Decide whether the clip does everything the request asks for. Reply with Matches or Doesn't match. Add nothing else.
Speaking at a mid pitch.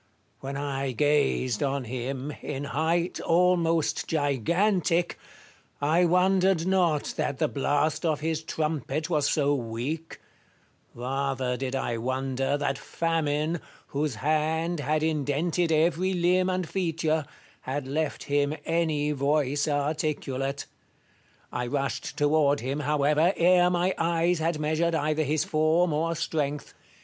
Matches